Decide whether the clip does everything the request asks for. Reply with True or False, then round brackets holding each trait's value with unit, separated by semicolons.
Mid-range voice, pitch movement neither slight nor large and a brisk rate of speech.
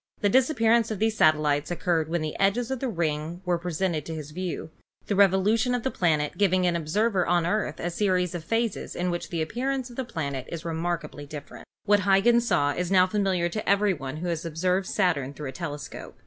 True (180 Hz; 4.5 semitones; 225 wpm)